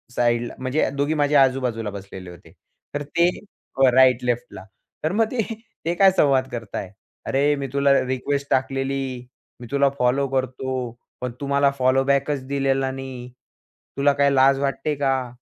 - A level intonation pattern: Yes, narrow, 1.8 semitones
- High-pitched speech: No, low, 135 Hz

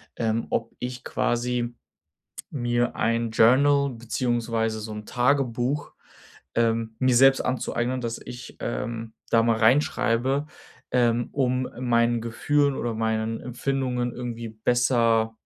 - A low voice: Yes, low, 120 Hz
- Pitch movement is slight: Yes, narrow, 1.9 semitones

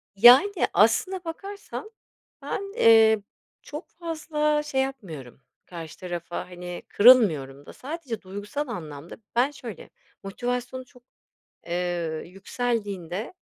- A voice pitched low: No, high, 225 Hz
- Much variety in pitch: Yes, wide, 8.5 semitones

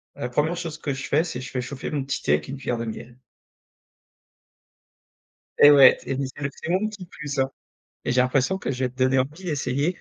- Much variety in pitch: No, average, 3.1 semitones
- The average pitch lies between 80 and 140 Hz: Yes, low, 135 Hz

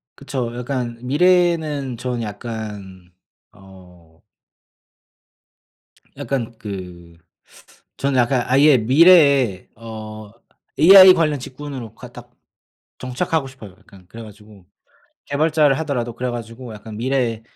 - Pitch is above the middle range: No, low, 120 Hz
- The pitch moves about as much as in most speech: Yes, average, 4.5 semitones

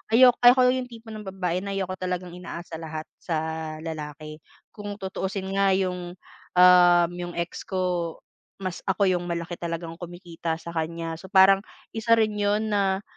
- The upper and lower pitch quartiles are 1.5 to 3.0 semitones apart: Yes, narrow, 2.6 semitones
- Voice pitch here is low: No, medium, 180 Hz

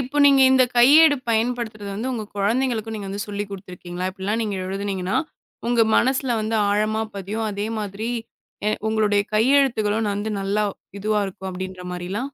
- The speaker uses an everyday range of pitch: Yes, average, 3.1 semitones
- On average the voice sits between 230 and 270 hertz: No, high, 215 Hz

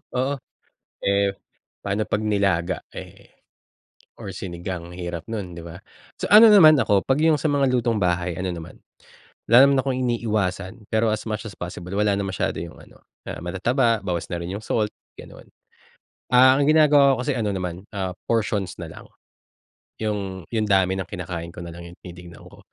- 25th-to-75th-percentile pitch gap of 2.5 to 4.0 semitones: No, average, 4.6 semitones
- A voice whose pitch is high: No, low, 100 Hz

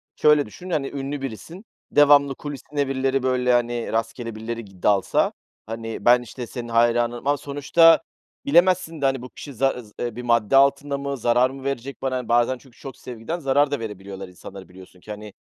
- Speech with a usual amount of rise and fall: Yes, average, 3.4 semitones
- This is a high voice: No, low, 125 Hz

